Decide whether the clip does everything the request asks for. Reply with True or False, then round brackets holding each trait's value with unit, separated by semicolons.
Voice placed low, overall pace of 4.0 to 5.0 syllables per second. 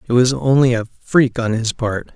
True (120 Hz; 4.9 syllables/s)